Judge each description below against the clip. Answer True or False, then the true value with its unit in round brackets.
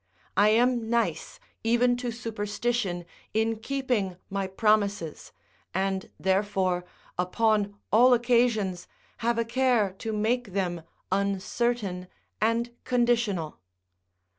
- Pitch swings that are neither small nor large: True (3.6 semitones)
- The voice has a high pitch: True (220 Hz)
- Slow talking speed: True (100 wpm)